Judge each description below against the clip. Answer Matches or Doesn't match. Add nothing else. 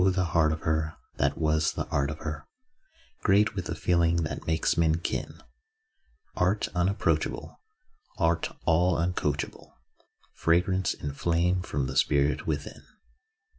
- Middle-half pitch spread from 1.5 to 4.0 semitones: Matches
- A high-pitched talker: Doesn't match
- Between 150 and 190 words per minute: Doesn't match